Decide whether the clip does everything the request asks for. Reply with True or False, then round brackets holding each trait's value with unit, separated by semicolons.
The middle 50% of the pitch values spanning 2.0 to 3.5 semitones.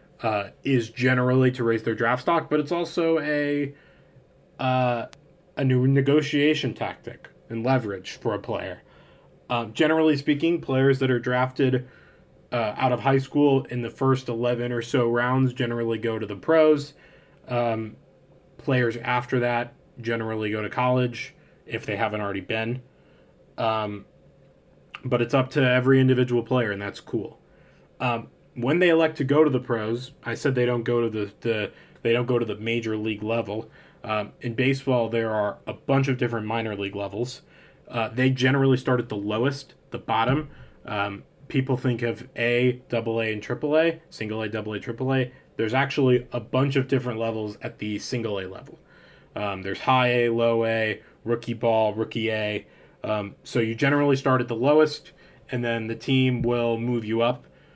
True (2.8 semitones)